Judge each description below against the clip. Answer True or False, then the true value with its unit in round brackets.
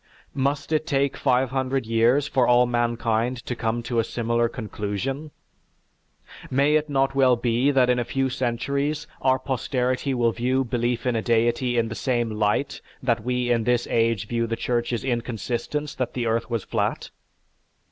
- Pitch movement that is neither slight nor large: False (2.2 semitones)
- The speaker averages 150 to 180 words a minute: True (170 wpm)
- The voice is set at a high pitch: False (120 Hz)